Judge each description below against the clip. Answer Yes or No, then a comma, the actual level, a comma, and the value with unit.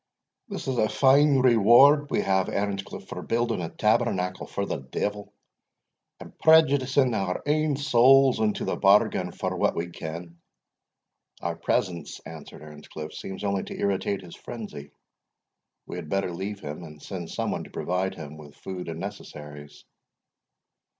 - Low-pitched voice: Yes, low, 100 Hz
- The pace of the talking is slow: No, average, 150 wpm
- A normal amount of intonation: No, wide, 6.3 semitones